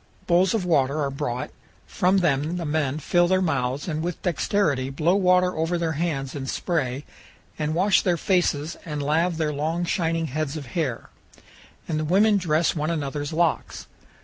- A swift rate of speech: No, average, 175 wpm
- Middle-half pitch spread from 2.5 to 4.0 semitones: Yes, average, 3.2 semitones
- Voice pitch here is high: No, medium, 160 Hz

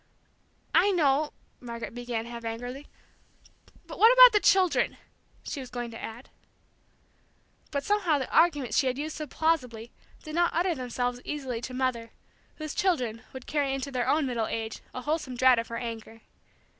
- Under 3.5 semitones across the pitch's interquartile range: No, average, 4.5 semitones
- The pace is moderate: Yes, average, 170 wpm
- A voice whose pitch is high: Yes, very high, 260 Hz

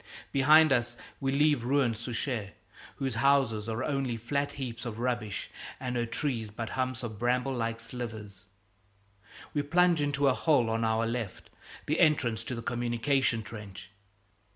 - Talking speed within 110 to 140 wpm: No, average, 155 wpm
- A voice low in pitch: Yes, low, 120 Hz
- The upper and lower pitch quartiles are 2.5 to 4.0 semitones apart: Yes, average, 3.4 semitones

